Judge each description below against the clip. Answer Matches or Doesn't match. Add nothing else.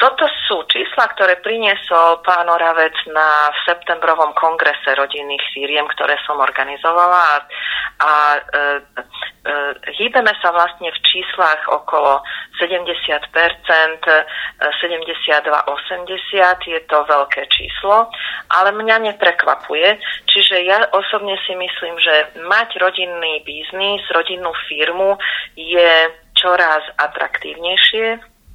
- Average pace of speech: Doesn't match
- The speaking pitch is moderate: Matches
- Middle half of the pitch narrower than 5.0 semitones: Matches